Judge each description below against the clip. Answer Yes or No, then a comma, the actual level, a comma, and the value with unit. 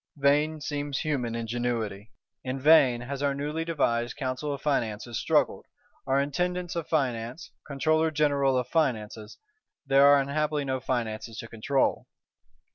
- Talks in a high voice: No, low, 135 Hz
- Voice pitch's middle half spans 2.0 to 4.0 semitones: Yes, average, 3.7 semitones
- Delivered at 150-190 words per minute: No, slow, 135 wpm